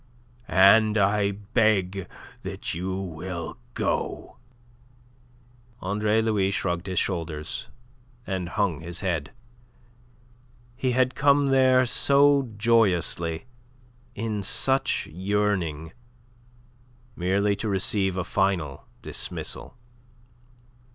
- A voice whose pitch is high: No, low, 100 Hz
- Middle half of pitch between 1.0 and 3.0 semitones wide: No, average, 3.7 semitones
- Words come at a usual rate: No, slow, 90 wpm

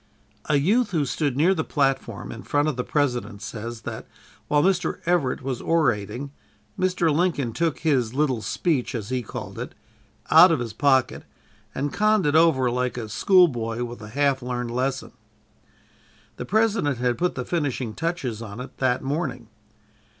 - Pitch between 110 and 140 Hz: Yes, low, 135 Hz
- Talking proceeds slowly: No, average, 165 wpm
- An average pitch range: Yes, average, 4.8 semitones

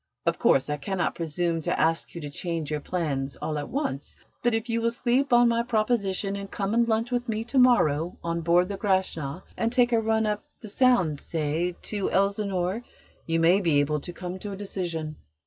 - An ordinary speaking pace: No, fast, 210 wpm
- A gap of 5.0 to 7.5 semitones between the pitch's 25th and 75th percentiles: Yes, wide, 5.5 semitones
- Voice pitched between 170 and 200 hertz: Yes, high, 190 Hz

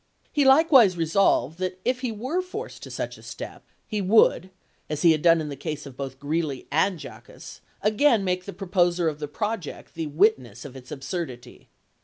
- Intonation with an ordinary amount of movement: No, wide, 6.1 semitones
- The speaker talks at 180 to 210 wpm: Yes, average, 190 wpm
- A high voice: No, medium, 175 Hz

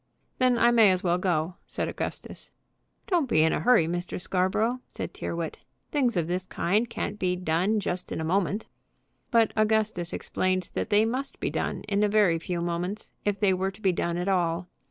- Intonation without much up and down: No, average, 3.7 semitones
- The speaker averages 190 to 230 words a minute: Yes, average, 195 wpm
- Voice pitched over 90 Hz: Yes, high, 190 Hz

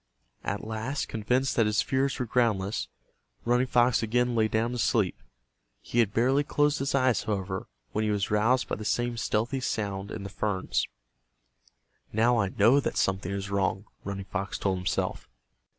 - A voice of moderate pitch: No, low, 110 Hz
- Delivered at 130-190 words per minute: Yes, average, 170 wpm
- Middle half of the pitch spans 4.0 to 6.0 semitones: No, average, 3.6 semitones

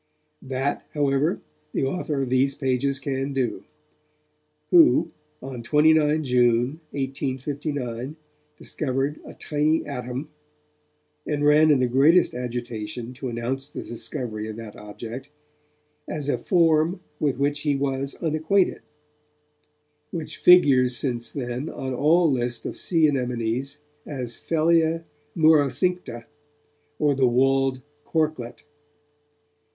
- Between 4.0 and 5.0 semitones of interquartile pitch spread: No, average, 3.6 semitones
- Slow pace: Yes, slow, 115 wpm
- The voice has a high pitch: No, low, 135 Hz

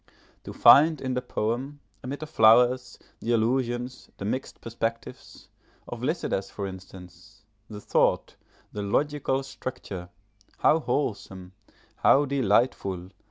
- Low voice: Yes, low, 120 Hz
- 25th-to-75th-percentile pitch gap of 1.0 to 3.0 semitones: No, average, 5.0 semitones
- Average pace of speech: No, slow, 115 wpm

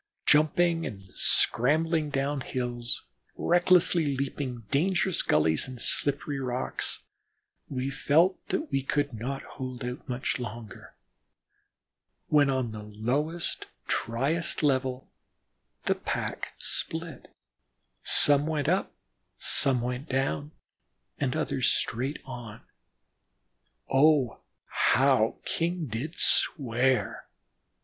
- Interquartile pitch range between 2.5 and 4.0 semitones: Yes, average, 3.6 semitones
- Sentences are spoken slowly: Yes, slow, 100 wpm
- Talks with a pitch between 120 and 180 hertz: Yes, low, 135 Hz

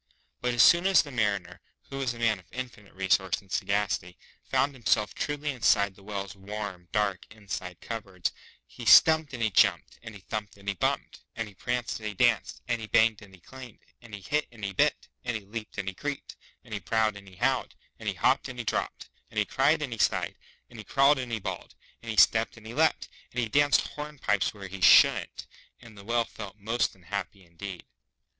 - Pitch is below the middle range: Yes, low, 110 Hz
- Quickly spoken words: Yes, fast, 220 wpm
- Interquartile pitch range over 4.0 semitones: No, average, 3.7 semitones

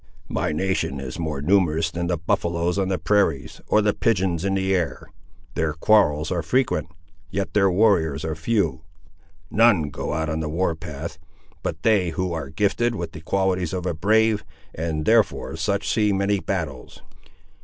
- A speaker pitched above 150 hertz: No, very low, 90 Hz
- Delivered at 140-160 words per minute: No, average, 170 wpm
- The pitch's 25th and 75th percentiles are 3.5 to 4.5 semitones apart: Yes, average, 4.0 semitones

